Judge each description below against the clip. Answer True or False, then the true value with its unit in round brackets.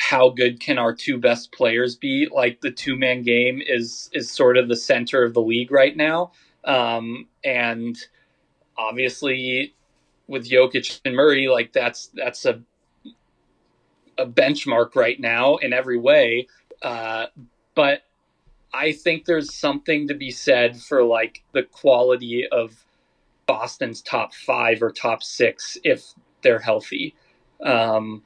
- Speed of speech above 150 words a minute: False (140 wpm)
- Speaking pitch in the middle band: False (125 Hz)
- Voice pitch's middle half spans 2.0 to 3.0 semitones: True (2.6 semitones)